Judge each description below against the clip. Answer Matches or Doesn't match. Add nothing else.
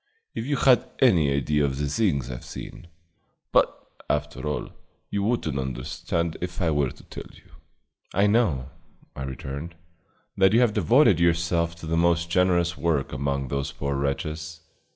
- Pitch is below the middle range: Matches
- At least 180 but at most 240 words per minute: Doesn't match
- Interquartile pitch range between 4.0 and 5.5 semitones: Matches